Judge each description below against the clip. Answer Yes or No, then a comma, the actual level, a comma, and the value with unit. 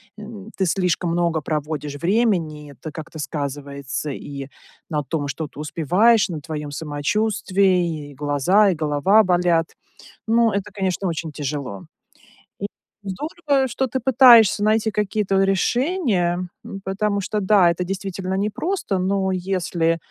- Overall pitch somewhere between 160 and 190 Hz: Yes, medium, 185 Hz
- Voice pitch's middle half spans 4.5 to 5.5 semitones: Yes, average, 5.2 semitones